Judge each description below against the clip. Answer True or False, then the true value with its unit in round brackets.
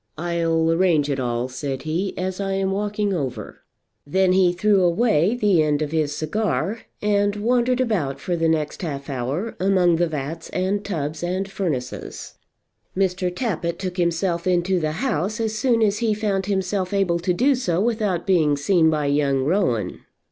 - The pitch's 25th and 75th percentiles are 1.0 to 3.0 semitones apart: False (4.5 semitones)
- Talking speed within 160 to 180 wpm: True (170 wpm)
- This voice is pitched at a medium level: True (180 Hz)